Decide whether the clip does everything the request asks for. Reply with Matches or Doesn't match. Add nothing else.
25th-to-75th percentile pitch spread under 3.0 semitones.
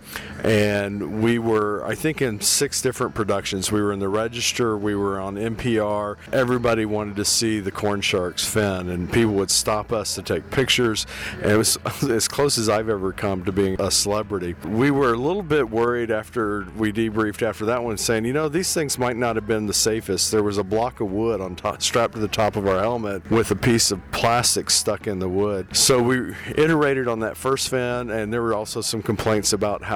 Matches